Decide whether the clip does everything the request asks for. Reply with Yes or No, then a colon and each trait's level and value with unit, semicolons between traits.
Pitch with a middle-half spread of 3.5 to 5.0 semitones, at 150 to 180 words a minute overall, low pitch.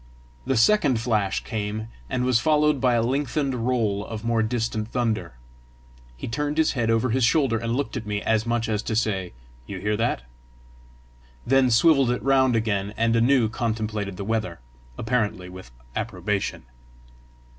No: average, 3.0 semitones; average, 160 wpm; low, 115 Hz